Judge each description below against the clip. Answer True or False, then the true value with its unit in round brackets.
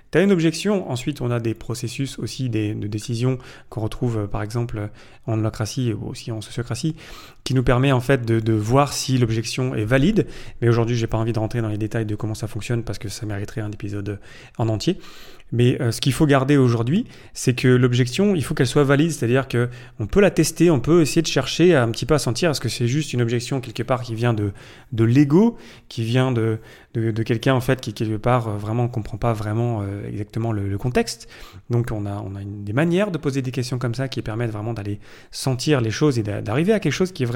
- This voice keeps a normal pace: False (240 wpm)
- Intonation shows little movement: False (3.6 semitones)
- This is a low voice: True (120 Hz)